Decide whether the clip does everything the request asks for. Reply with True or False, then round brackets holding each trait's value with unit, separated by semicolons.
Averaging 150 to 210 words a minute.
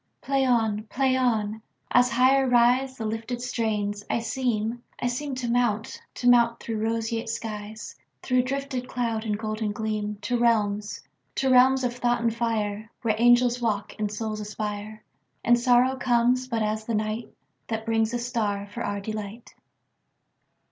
False (140 wpm)